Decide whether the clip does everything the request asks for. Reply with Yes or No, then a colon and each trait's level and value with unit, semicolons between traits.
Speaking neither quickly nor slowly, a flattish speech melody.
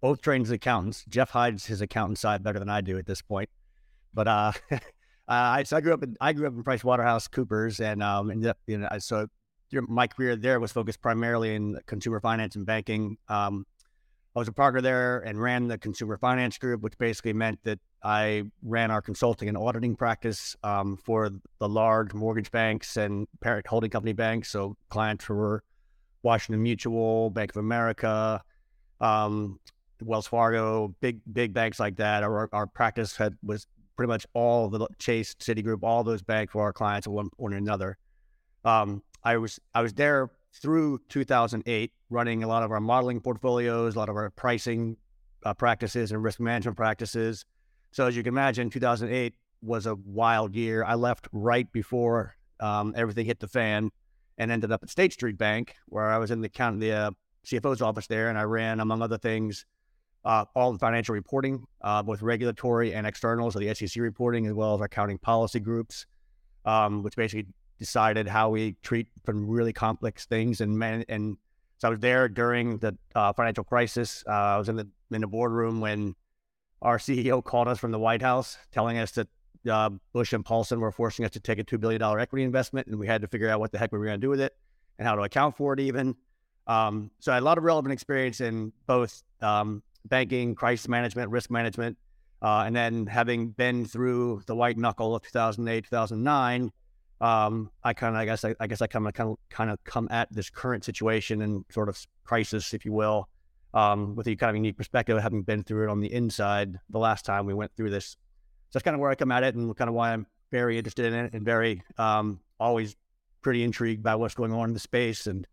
No: fast, 210 wpm; narrow, 2.0 semitones